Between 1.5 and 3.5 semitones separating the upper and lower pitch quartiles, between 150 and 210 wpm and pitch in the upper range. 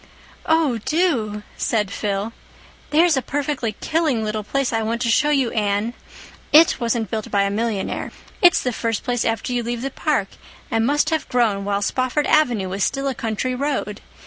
No: average, 4.5 semitones; average, 180 wpm; high, 235 Hz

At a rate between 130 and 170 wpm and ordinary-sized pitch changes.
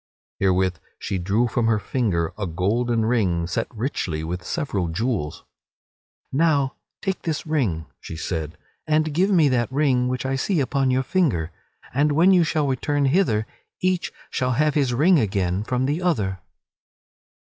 No: average, 160 wpm; wide, 7.7 semitones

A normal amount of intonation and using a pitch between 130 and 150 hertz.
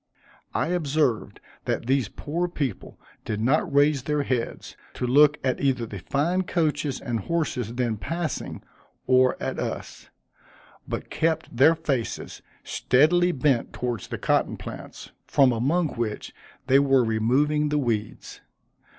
Yes: average, 4.0 semitones; medium, 140 Hz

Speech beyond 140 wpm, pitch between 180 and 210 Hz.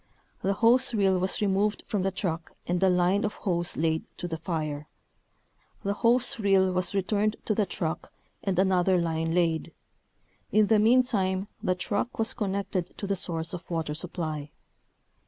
Yes: average, 170 wpm; high, 190 Hz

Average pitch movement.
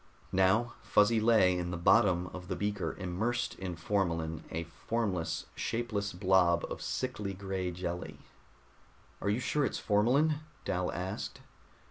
Yes: average, 3.7 semitones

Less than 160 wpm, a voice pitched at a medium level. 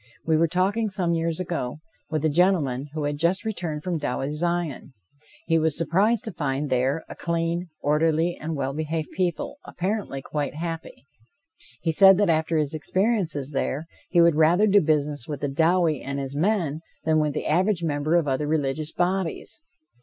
No: average, 175 wpm; medium, 160 Hz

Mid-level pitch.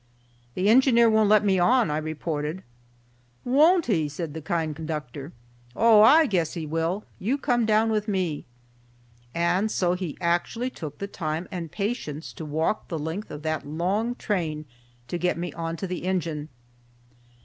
Yes: medium, 175 Hz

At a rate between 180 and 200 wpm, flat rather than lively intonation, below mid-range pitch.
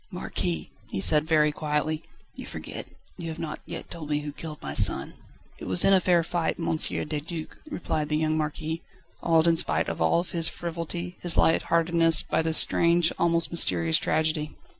No: average, 185 wpm; narrow, 1.8 semitones; medium, 160 Hz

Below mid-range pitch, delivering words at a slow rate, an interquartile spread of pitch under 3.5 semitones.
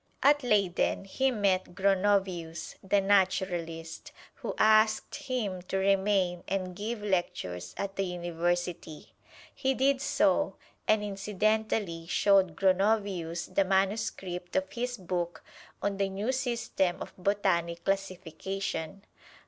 No: high, 195 Hz; slow, 115 wpm; average, 2.7 semitones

